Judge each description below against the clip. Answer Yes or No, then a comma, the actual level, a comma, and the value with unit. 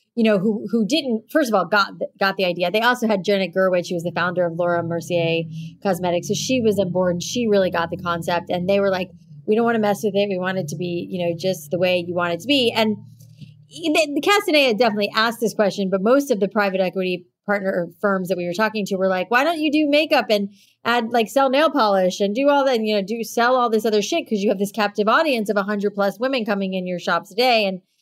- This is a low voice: No, high, 205 Hz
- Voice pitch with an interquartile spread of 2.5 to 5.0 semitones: Yes, average, 4.1 semitones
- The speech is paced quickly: Yes, fast, 270 wpm